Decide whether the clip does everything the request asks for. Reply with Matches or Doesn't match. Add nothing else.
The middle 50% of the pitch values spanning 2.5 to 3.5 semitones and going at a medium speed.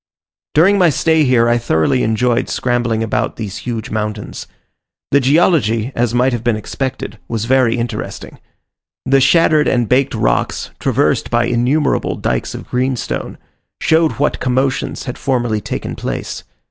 Matches